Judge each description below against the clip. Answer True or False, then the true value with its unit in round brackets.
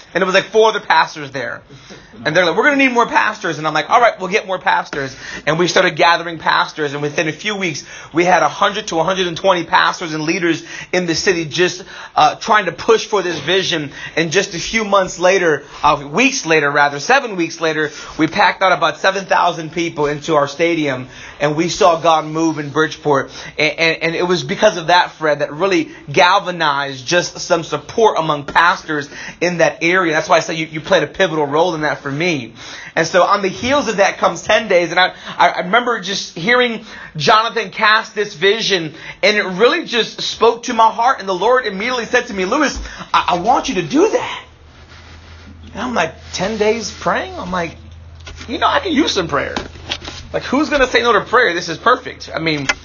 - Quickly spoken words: True (225 wpm)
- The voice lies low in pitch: False (175 Hz)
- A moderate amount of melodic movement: True (4.7 semitones)